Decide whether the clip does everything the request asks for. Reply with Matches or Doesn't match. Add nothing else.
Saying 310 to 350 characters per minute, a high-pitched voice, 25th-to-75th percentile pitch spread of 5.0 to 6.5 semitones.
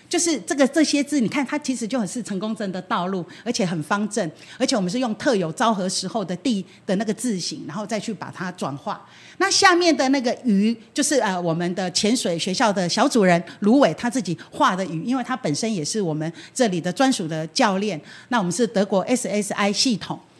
Matches